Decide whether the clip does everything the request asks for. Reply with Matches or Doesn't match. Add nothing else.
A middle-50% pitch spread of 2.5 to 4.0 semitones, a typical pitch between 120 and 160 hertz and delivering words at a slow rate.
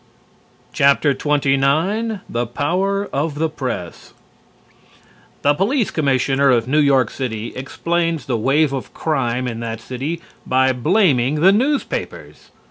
Doesn't match